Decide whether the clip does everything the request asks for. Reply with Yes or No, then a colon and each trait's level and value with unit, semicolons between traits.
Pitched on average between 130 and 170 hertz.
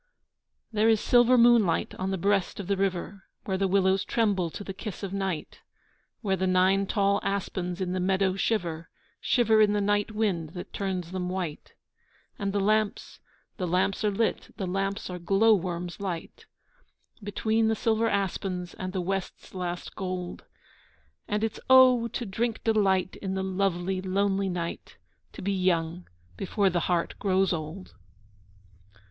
No: high, 195 Hz